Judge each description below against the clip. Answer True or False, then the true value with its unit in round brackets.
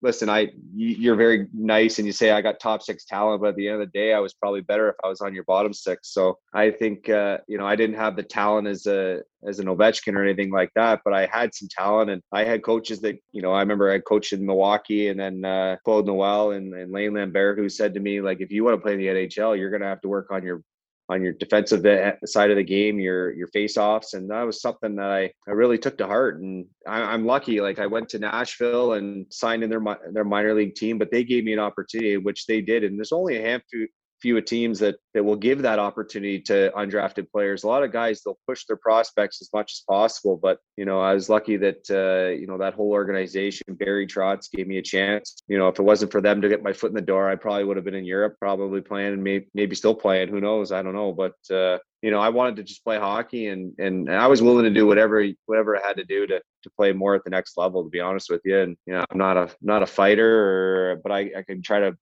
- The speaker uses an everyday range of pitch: False (1.9 semitones)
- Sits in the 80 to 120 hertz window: True (100 Hz)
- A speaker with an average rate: False (270 wpm)